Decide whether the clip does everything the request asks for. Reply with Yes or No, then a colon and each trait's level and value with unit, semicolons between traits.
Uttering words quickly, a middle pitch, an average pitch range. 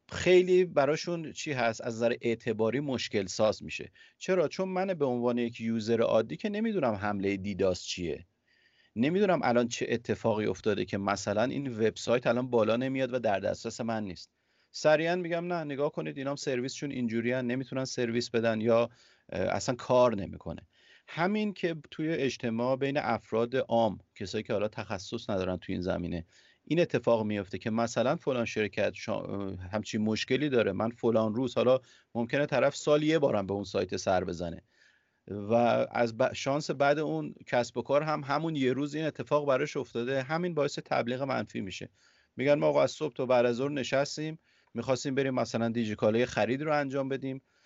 No: fast, 170 wpm; low, 125 Hz; average, 4.2 semitones